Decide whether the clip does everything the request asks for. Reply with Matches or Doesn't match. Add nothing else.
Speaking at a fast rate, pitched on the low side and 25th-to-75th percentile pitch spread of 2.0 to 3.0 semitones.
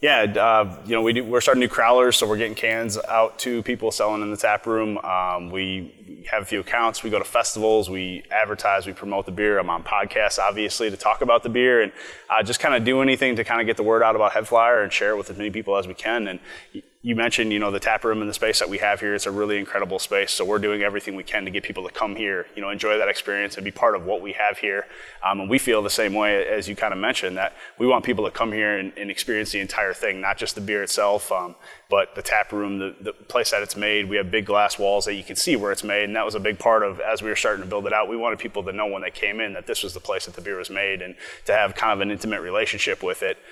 Matches